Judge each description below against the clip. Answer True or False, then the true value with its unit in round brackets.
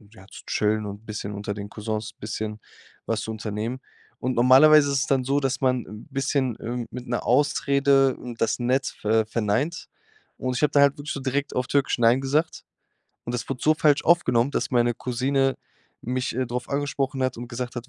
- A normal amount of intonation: True (3.2 semitones)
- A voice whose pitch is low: True (125 Hz)